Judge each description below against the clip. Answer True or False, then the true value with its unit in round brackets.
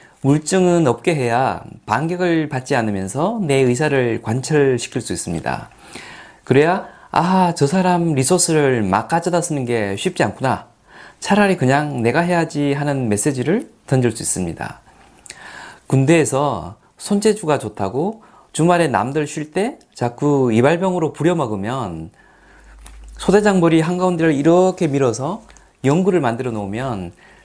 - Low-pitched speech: False (145 Hz)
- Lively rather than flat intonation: True (6.5 semitones)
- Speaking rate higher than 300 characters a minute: False (285 characters per minute)